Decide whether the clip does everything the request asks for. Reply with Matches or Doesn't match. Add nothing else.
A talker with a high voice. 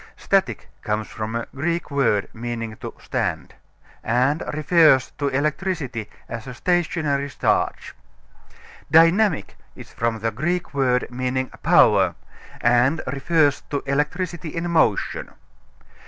Doesn't match